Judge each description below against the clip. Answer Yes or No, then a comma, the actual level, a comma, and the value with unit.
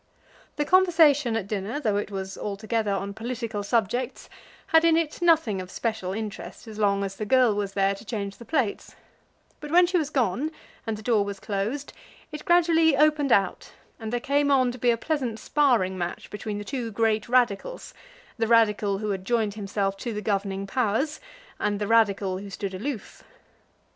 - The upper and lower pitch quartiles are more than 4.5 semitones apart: Yes, average, 5.1 semitones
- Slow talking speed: No, average, 185 wpm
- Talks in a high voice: Yes, high, 220 Hz